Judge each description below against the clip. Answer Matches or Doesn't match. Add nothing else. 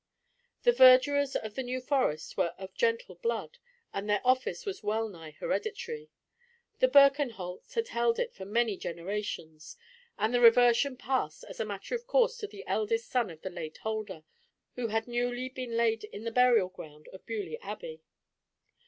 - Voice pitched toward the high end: Matches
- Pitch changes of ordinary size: Doesn't match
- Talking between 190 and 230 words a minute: Doesn't match